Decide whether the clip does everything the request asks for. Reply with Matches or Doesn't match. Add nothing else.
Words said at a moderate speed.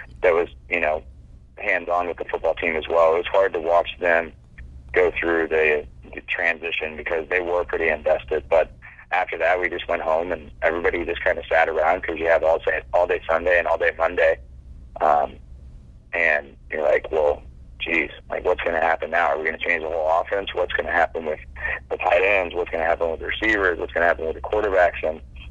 Doesn't match